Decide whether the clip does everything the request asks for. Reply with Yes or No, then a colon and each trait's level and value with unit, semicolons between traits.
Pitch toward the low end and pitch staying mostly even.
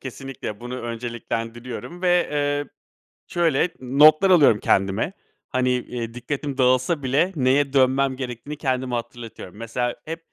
No: low, 130 Hz; average, 3.2 semitones